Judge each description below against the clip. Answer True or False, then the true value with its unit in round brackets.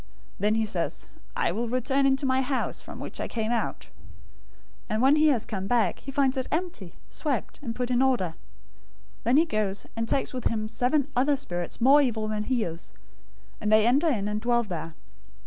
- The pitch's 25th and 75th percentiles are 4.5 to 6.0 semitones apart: False (4.0 semitones)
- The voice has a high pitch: True (240 Hz)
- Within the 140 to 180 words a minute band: False (205 wpm)